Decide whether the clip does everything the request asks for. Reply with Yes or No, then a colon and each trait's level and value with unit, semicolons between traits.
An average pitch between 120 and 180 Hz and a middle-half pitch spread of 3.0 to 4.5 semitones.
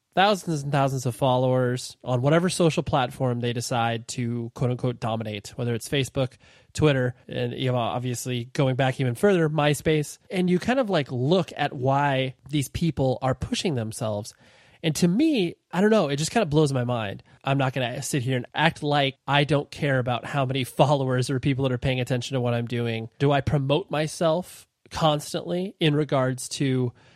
Yes: low, 135 Hz; average, 3.4 semitones